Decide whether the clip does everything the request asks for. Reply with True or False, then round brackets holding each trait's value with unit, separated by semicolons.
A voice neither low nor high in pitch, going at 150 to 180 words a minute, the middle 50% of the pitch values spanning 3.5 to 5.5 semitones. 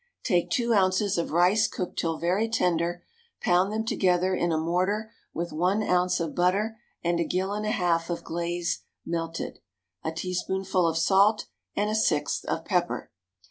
False (180 Hz; 170 wpm; 3.1 semitones)